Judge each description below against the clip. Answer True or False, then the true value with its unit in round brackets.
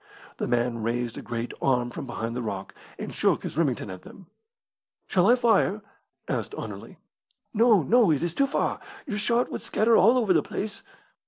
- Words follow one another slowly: False (185 wpm)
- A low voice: False (165 Hz)